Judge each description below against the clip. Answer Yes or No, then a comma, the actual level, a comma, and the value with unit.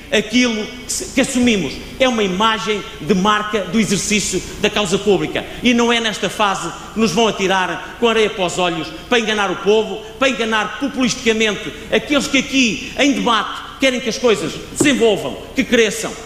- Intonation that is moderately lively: Yes, average, 3.3 semitones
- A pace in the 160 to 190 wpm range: Yes, average, 170 wpm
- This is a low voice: No, high, 220 Hz